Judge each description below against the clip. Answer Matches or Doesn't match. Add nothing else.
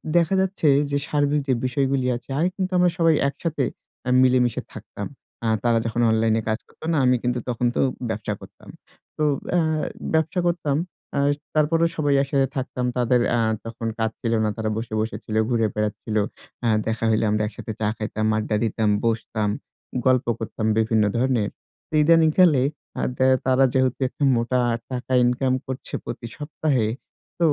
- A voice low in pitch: Matches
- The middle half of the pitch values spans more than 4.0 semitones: Matches